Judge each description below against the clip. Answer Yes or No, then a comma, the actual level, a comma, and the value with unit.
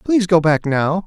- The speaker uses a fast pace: Yes, fast, 225 wpm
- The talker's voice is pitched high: No, medium, 175 Hz